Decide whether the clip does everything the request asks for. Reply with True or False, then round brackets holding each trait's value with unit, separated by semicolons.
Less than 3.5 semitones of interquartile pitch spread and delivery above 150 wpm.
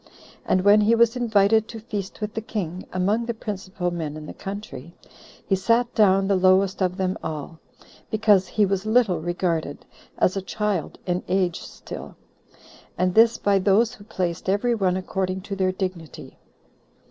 True (2.7 semitones; 170 wpm)